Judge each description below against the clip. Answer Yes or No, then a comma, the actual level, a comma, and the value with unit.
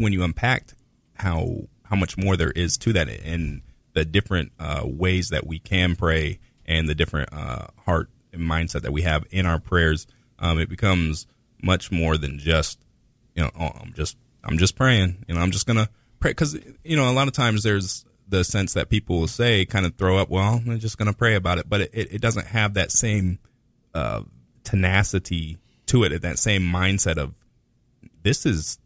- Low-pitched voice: Yes, very low, 95 Hz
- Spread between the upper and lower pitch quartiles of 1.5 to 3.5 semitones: No, average, 5.2 semitones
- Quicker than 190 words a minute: Yes, average, 200 wpm